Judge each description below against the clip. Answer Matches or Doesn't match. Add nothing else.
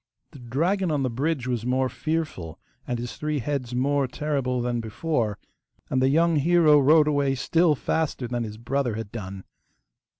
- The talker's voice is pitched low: Matches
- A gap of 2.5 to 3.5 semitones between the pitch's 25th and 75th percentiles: Doesn't match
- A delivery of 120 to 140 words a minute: Doesn't match